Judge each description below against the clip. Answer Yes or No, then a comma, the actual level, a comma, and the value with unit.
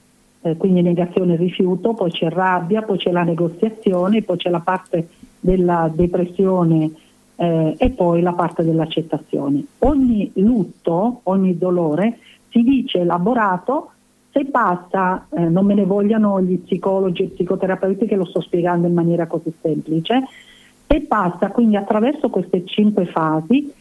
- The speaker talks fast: No, average, 145 wpm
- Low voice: No, medium, 185 Hz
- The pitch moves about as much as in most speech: Yes, average, 3.9 semitones